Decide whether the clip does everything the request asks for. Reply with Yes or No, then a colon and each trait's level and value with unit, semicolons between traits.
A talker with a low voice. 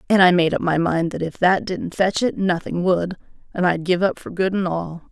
No: medium, 180 Hz